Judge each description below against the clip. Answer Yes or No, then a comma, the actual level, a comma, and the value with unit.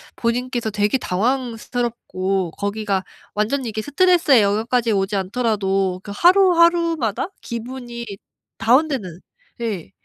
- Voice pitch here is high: Yes, high, 230 Hz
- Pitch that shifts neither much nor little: Yes, average, 4.6 semitones